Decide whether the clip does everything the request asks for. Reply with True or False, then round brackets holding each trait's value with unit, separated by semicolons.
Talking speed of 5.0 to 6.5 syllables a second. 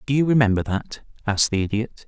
True (6.3 syllables/s)